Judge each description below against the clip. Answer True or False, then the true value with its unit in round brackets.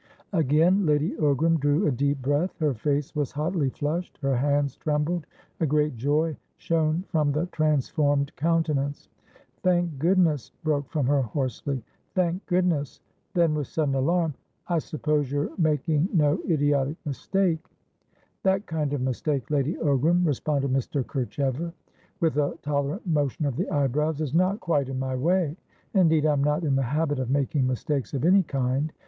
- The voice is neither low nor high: True (150 Hz)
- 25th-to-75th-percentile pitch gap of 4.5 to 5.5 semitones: False (2.8 semitones)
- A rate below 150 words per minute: False (155 wpm)